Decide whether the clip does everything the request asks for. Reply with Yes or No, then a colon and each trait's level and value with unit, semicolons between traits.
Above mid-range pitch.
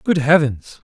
No: medium, 140 Hz